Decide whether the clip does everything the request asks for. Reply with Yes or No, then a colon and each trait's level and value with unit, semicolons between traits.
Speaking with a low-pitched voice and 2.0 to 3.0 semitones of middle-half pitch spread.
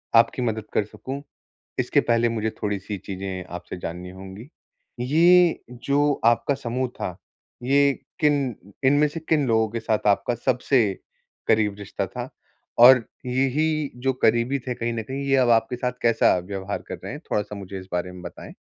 No: low, 120 Hz; average, 4.7 semitones